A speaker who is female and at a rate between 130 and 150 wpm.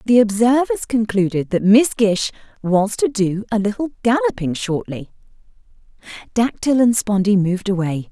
Yes: female; slow, 135 wpm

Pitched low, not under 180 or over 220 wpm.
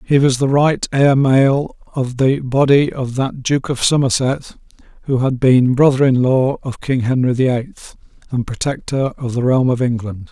Yes: low, 130 Hz; average, 185 wpm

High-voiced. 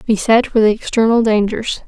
Yes: high, 220 Hz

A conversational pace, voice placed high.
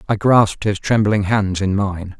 No: average, 190 wpm; low, 100 Hz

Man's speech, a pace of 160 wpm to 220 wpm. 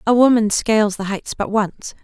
No: female; fast, 205 wpm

